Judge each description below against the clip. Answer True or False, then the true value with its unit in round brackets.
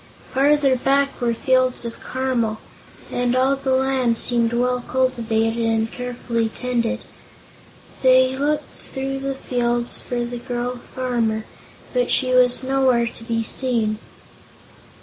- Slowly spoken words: True (130 wpm)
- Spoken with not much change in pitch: True (1.9 semitones)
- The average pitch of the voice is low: False (250 Hz)